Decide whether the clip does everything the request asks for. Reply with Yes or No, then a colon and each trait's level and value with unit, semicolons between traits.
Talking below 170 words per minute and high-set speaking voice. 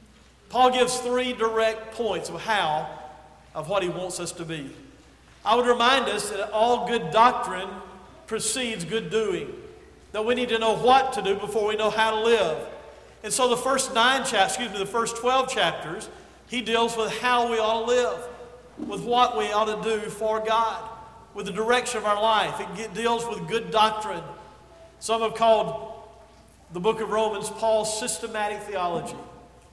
No: average, 180 wpm; high, 220 Hz